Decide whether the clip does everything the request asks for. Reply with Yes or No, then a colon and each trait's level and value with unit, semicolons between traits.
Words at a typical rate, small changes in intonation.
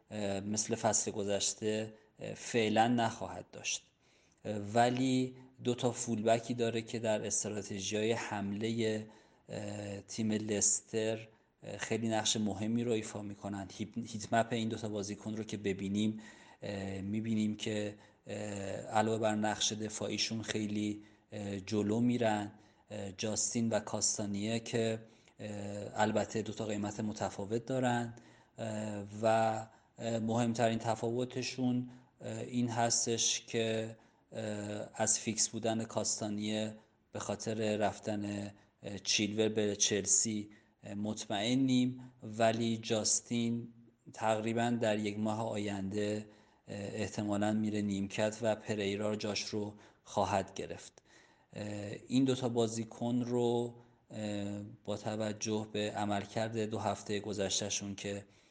No: slow, 100 wpm; narrow, 1.6 semitones